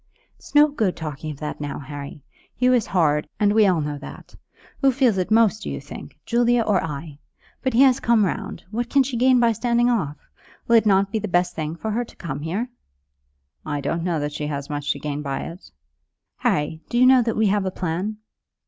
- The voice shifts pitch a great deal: Yes, wide, 7.8 semitones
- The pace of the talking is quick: Yes, fast, 230 wpm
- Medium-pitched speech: No, high, 195 Hz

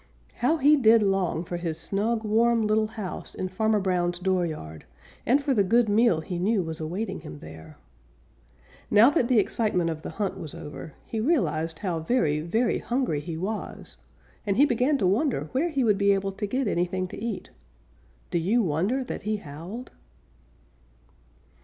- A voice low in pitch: No, high, 200 Hz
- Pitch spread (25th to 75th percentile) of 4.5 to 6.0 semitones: Yes, average, 5.3 semitones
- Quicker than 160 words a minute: Yes, average, 175 wpm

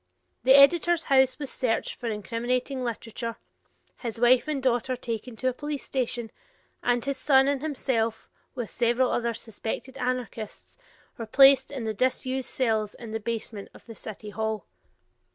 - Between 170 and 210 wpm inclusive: No, average, 155 wpm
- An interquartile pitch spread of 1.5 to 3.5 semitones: Yes, average, 2.8 semitones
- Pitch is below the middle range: No, high, 245 Hz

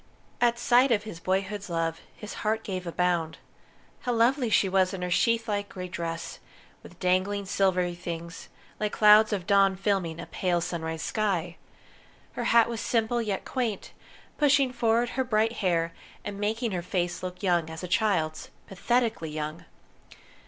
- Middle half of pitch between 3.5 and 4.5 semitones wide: Yes, average, 4.1 semitones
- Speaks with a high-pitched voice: Yes, high, 195 Hz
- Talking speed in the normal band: Yes, average, 160 wpm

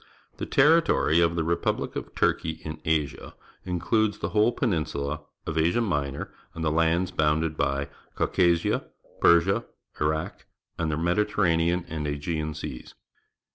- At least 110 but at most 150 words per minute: Yes, slow, 135 wpm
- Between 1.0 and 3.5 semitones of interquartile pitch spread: Yes, narrow, 2.6 semitones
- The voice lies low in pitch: Yes, very low, 80 Hz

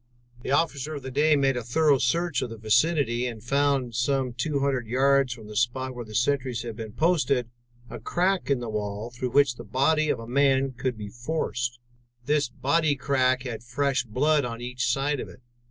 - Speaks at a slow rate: No, average, 200 wpm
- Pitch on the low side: Yes, low, 130 Hz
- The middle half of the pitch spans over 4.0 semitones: No, average, 3.0 semitones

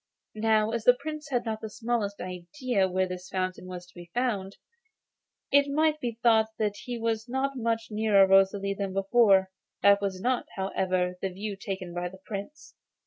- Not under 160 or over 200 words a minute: Yes, average, 180 wpm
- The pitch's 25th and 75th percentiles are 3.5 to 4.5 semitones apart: Yes, average, 3.8 semitones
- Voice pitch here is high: Yes, high, 205 Hz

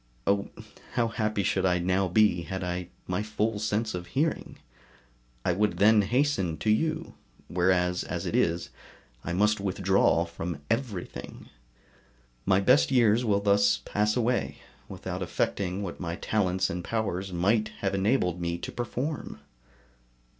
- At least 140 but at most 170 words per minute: Yes, average, 145 wpm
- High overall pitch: No, low, 100 Hz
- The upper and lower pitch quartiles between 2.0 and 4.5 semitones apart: Yes, average, 3.4 semitones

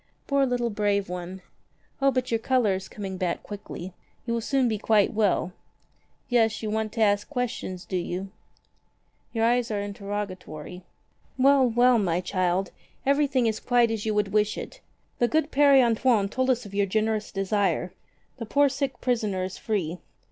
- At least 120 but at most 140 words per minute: No, average, 170 wpm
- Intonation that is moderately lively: Yes, average, 4.1 semitones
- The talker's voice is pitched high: Yes, high, 215 Hz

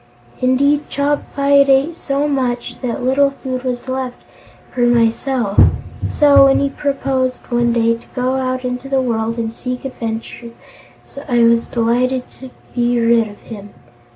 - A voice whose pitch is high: Yes, very high, 255 Hz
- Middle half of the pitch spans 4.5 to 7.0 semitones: No, narrow, 2.5 semitones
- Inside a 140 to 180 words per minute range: Yes, average, 150 wpm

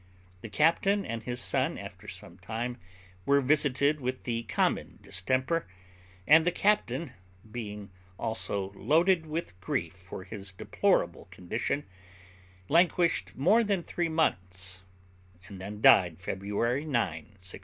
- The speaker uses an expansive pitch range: Yes, wide, 8.4 semitones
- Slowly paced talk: Yes, slow, 125 wpm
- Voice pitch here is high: No, low, 120 Hz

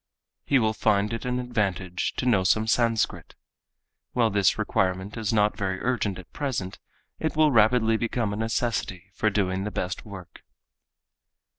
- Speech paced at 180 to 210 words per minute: No, average, 155 wpm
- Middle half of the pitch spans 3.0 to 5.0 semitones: Yes, average, 3.5 semitones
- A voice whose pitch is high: No, low, 110 Hz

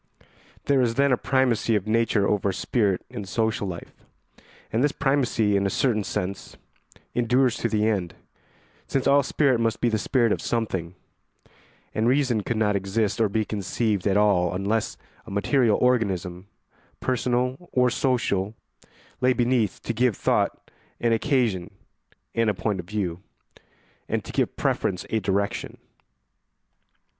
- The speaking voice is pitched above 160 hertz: No, low, 110 Hz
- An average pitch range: Yes, average, 3.9 semitones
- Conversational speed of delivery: Yes, average, 150 wpm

